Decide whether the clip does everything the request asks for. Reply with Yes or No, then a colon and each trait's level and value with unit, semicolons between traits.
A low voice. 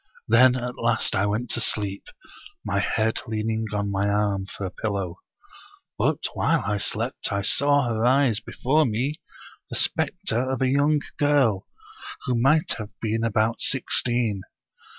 Yes: low, 115 Hz